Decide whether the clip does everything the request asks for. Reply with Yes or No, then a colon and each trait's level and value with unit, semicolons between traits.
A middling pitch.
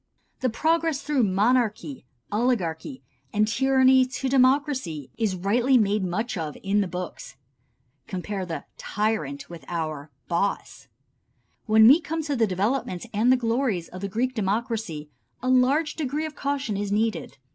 No: high, 220 Hz